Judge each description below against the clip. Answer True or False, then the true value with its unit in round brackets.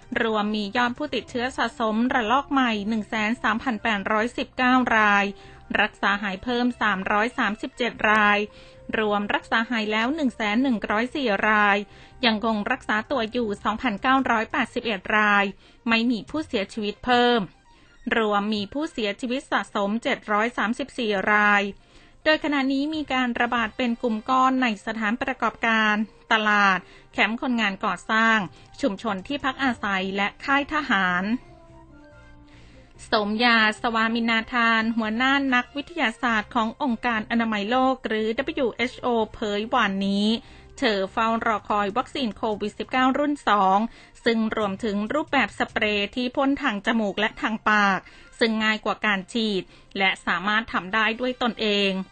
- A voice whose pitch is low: False (225 Hz)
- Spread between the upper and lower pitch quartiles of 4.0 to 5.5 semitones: False (3.1 semitones)